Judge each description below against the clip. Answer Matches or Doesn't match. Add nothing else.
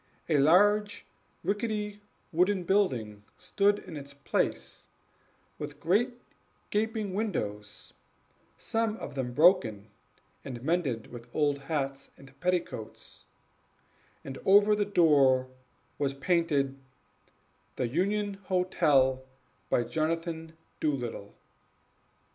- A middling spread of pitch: Doesn't match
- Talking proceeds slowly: Matches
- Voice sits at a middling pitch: Matches